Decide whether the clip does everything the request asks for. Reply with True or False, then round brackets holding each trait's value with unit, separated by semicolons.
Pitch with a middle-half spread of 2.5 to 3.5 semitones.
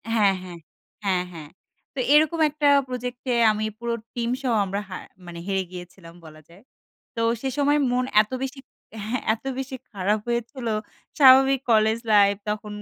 False (5.0 semitones)